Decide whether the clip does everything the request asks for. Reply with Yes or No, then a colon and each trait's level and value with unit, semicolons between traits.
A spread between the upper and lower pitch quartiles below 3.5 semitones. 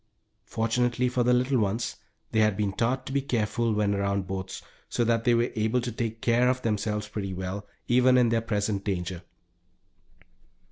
Yes: average, 3.1 semitones